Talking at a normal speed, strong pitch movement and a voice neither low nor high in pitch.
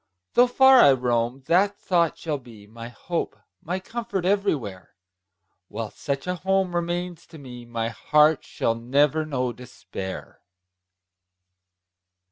No: slow, 125 wpm; wide, 7.1 semitones; medium, 150 Hz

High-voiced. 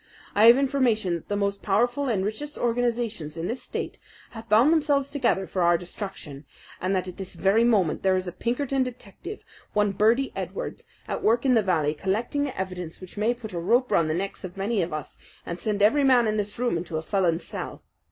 Yes: high, 210 Hz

